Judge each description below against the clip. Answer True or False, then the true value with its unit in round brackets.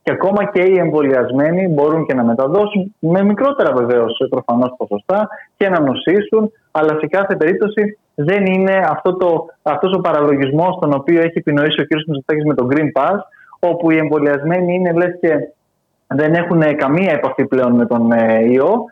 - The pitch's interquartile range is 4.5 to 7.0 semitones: True (4.9 semitones)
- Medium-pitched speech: True (155 Hz)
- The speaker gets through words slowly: False (165 wpm)